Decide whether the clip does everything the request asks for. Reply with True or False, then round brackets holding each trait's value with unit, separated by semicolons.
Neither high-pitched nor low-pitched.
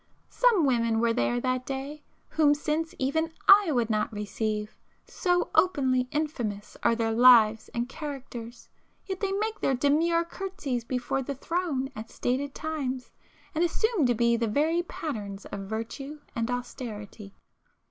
False (260 Hz)